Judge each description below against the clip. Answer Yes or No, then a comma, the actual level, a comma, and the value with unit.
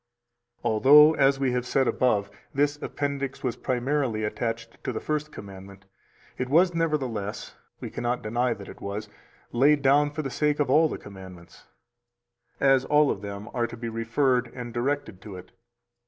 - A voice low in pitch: Yes, low, 125 Hz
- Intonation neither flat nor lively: Yes, average, 5.0 semitones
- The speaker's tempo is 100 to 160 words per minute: No, average, 170 wpm